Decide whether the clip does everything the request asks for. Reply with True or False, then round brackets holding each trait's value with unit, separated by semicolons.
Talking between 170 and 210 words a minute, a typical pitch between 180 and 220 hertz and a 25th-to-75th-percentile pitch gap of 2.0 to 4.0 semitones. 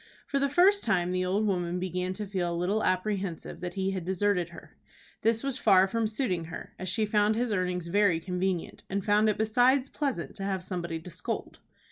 True (205 wpm; 190 Hz; 3.1 semitones)